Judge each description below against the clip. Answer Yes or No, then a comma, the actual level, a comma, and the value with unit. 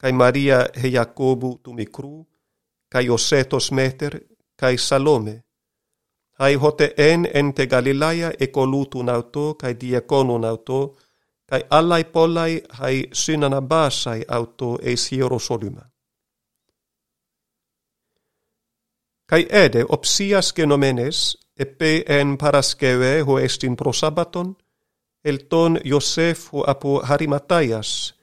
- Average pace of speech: No, slow, 100 wpm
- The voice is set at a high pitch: No, medium, 140 Hz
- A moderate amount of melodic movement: Yes, average, 3.4 semitones